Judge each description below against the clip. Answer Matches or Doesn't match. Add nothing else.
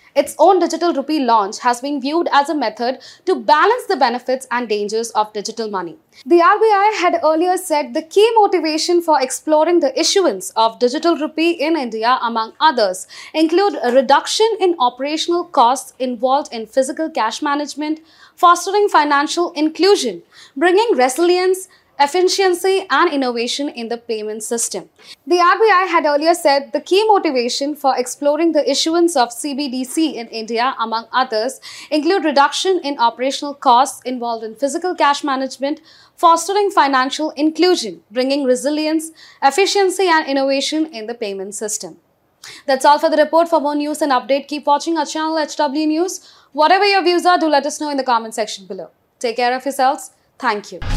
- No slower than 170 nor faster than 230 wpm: Doesn't match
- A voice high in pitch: Matches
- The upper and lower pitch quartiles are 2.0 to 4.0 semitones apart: Doesn't match